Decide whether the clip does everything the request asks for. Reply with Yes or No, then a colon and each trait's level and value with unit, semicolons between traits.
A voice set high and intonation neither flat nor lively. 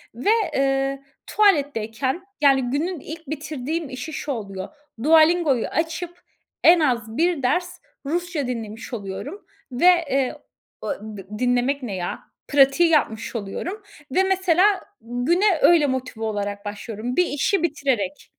No: very high, 275 Hz; wide, 5.7 semitones